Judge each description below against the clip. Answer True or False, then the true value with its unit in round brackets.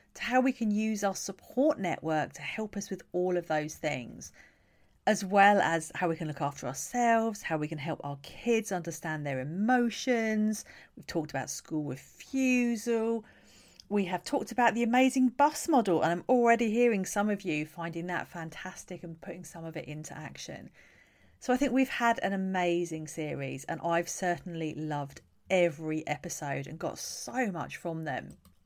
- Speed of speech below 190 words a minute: True (175 wpm)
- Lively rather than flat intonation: True (6.3 semitones)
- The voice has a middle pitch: True (175 Hz)